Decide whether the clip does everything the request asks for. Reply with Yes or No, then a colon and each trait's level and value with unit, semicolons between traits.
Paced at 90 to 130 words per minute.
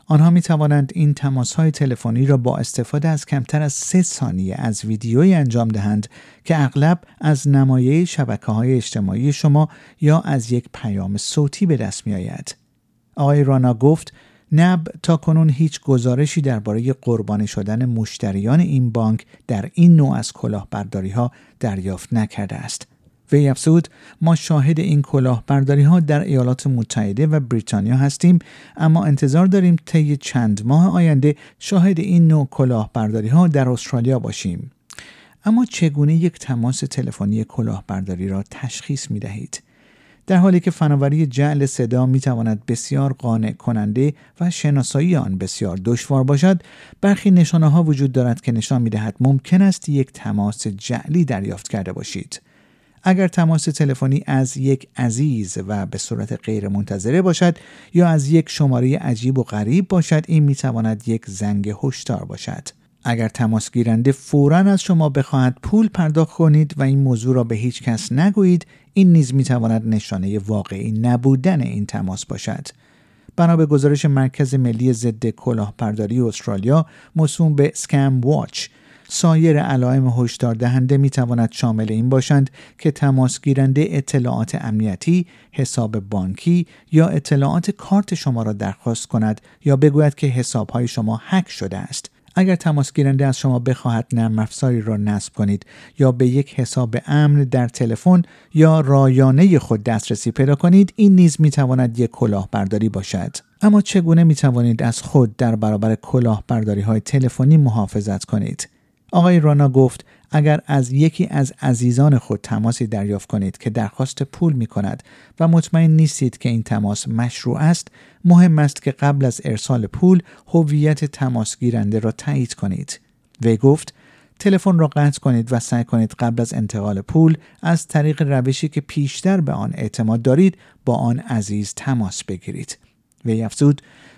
No: average, 150 wpm